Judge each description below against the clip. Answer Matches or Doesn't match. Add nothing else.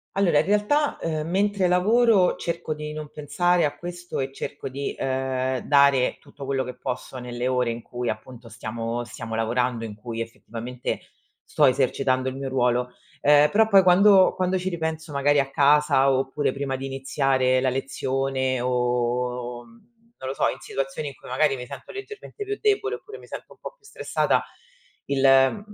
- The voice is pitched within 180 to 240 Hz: Doesn't match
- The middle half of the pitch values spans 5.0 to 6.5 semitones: Matches